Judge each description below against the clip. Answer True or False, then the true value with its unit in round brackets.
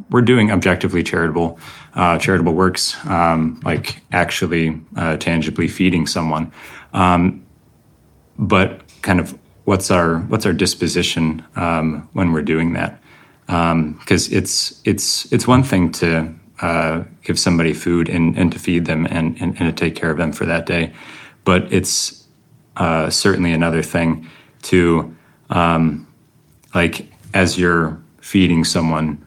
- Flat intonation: True (2.1 semitones)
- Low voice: True (85 Hz)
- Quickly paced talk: False (140 wpm)